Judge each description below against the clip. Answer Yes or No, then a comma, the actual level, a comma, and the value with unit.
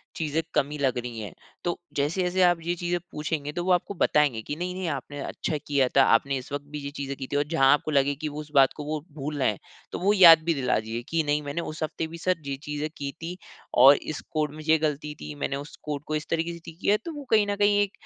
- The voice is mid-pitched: Yes, medium, 150 Hz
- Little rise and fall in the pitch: No, average, 3.3 semitones